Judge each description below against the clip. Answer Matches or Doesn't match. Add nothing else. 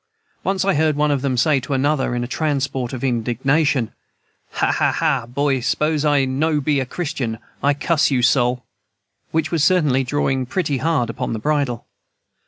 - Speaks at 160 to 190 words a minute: Matches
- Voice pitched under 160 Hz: Matches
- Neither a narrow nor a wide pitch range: Matches